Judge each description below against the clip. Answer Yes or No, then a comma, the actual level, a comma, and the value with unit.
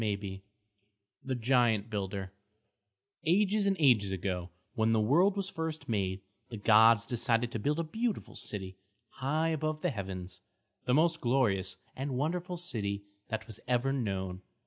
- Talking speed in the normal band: Yes, average, 150 wpm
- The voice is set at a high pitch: No, low, 120 Hz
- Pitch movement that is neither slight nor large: No, wide, 7.5 semitones